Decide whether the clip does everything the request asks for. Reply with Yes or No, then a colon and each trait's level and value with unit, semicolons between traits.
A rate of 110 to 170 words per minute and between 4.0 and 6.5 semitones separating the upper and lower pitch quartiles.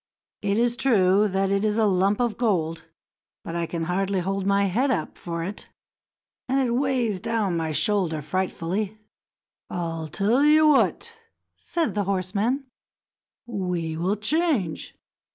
Yes: average, 145 wpm; average, 4.6 semitones